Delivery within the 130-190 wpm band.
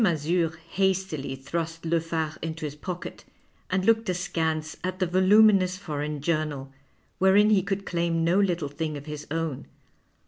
Yes: average, 150 wpm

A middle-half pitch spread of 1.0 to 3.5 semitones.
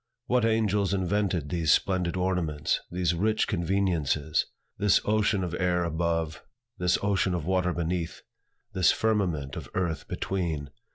Yes: average, 2.9 semitones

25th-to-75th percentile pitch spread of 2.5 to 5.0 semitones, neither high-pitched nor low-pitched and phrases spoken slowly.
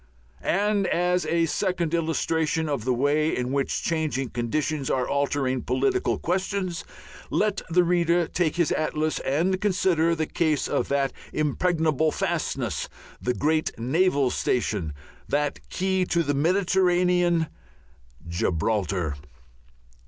Yes: average, 4.4 semitones; medium, 160 Hz; slow, 120 wpm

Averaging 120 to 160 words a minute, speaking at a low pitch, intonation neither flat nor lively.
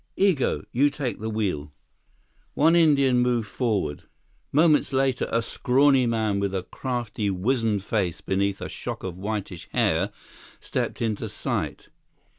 Yes: slow, 135 wpm; low, 115 Hz; average, 5.0 semitones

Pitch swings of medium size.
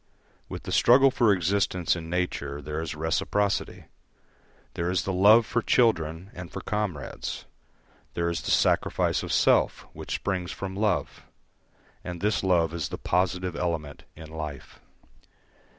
Yes: average, 3.7 semitones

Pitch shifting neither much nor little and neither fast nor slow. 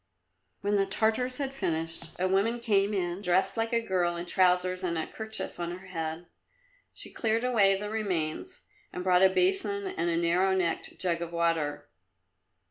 Yes: average, 4.2 semitones; average, 175 wpm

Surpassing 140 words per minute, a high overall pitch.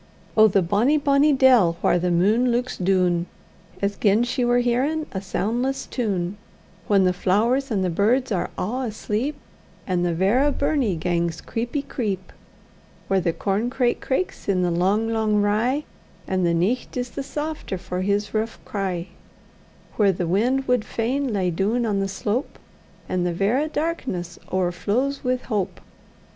Yes: average, 160 wpm; high, 210 Hz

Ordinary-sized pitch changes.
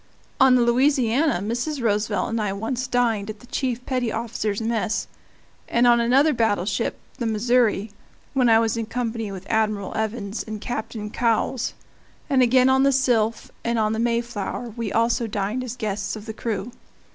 No: narrow, 2.3 semitones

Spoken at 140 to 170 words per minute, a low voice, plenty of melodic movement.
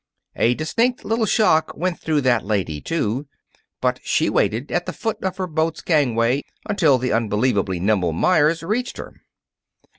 No: average, 155 wpm; medium, 145 Hz; wide, 7.6 semitones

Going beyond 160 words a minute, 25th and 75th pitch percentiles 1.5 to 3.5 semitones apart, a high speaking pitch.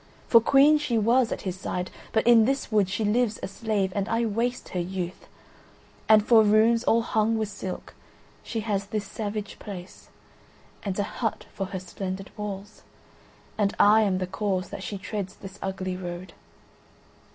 Yes: average, 175 wpm; average, 2.7 semitones; high, 205 Hz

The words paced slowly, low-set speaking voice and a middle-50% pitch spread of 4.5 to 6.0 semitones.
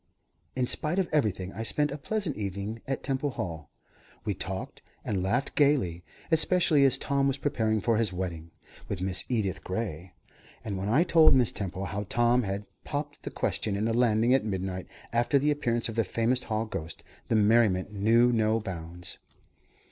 No: average, 180 wpm; low, 110 Hz; wide, 5.5 semitones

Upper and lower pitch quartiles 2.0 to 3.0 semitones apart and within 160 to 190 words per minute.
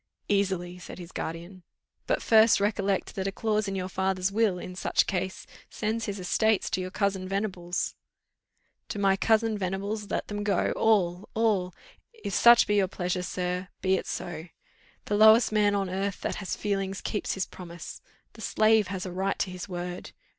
Yes: narrow, 2.4 semitones; average, 180 wpm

